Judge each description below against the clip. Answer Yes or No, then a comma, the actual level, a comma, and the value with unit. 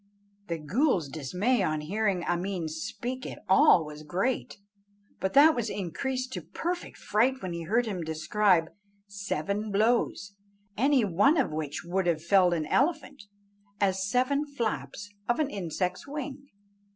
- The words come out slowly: No, average, 145 wpm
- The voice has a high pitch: Yes, high, 200 Hz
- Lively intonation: Yes, wide, 6.9 semitones